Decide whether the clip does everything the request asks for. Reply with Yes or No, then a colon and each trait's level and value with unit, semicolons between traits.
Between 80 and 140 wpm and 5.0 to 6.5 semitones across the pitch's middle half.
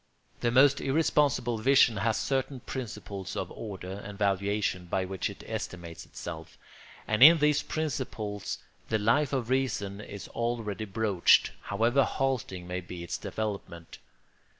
Yes: slow, 135 wpm; average, 5.3 semitones